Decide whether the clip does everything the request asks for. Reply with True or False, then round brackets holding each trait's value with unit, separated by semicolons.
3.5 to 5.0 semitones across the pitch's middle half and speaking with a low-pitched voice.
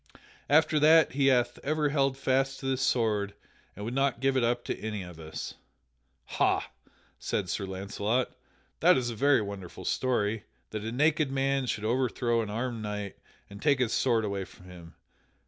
True (4.6 semitones; 120 Hz)